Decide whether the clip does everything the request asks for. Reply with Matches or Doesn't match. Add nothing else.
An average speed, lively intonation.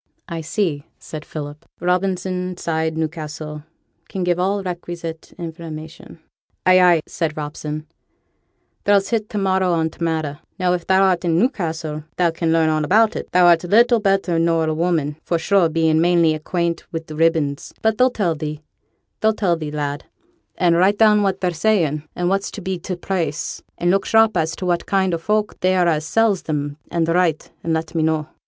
Doesn't match